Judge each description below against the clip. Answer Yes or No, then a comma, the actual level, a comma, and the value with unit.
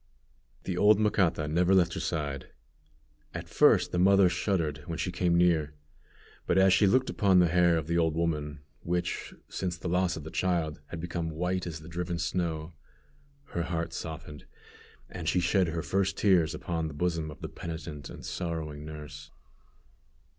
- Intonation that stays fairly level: Yes, narrow, 2.3 semitones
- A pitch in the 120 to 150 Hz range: No, very low, 85 Hz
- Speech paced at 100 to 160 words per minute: No, average, 175 wpm